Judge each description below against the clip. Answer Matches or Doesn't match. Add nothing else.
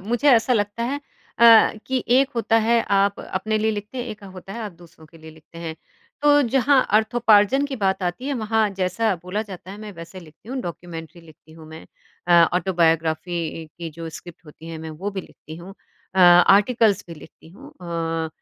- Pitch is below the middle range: Doesn't match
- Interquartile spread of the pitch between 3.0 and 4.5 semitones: Doesn't match